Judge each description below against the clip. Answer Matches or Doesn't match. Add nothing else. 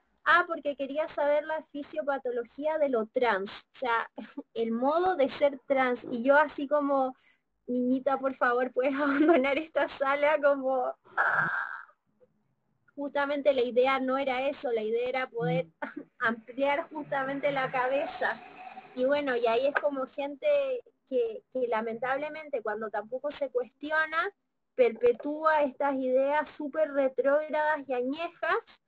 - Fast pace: Doesn't match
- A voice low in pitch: Doesn't match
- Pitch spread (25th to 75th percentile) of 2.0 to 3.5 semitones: Matches